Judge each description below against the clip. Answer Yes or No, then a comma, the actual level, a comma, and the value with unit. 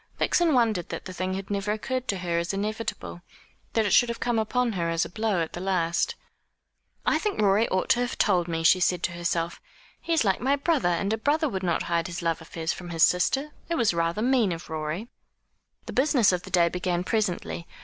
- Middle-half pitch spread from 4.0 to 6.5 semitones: Yes, average, 5.1 semitones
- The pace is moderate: No, fast, 225 wpm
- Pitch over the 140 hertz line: Yes, high, 190 Hz